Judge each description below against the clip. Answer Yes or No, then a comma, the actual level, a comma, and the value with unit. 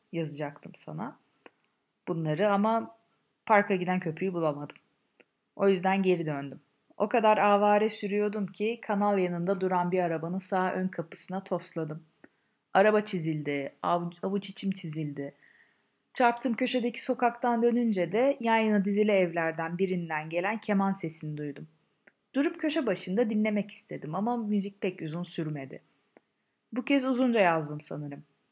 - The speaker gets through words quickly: No, average, 125 wpm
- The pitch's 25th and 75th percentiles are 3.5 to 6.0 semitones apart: Yes, average, 4.6 semitones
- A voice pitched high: Yes, high, 195 Hz